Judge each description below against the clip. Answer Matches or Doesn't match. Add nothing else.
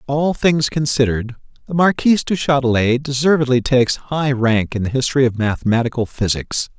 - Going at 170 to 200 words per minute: Doesn't match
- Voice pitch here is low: Matches